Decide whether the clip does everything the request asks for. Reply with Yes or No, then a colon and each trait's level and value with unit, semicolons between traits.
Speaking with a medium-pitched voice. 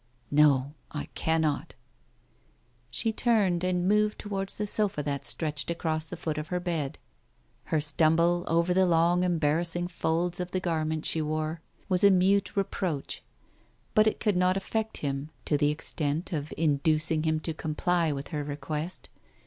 Yes: medium, 165 Hz